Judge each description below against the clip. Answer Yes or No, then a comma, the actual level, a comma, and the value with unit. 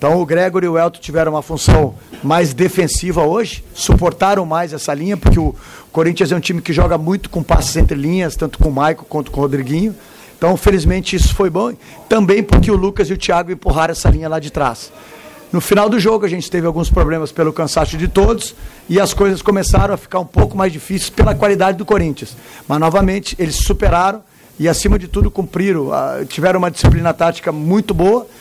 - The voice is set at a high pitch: No, medium, 175 Hz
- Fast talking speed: Yes, fast, 205 wpm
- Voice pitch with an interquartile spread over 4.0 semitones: No, average, 3.5 semitones